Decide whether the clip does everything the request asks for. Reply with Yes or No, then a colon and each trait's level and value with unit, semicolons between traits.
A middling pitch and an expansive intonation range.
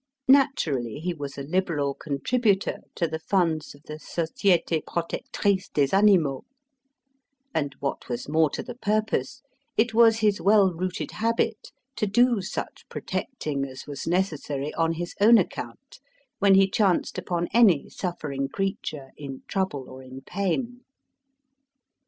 Yes: medium, 175 Hz; wide, 6.2 semitones